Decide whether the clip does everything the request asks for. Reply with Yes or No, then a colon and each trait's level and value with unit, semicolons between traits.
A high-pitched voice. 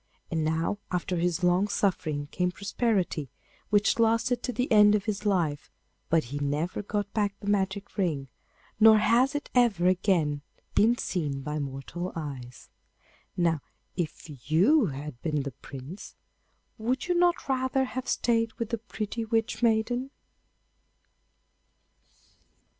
Yes: high, 195 Hz